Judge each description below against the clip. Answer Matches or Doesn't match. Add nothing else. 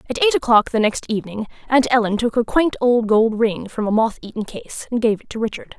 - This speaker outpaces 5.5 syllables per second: Matches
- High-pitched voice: Matches